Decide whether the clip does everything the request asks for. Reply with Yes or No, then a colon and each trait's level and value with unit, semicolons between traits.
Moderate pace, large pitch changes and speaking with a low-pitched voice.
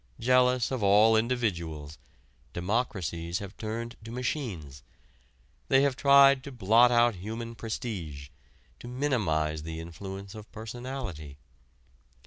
No: slow, 115 wpm; wide, 6.4 semitones; low, 110 Hz